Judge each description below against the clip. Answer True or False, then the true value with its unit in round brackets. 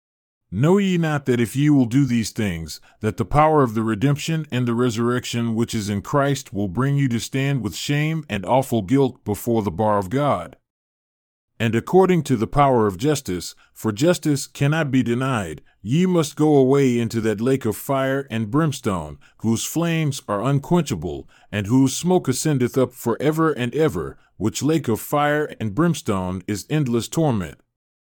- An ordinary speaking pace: True (175 wpm)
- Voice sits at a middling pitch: False (130 Hz)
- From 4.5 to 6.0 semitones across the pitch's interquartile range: True (4.8 semitones)